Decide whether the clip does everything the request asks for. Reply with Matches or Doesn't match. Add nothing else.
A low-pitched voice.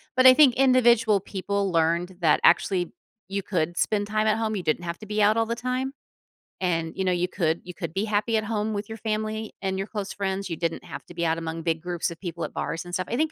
Doesn't match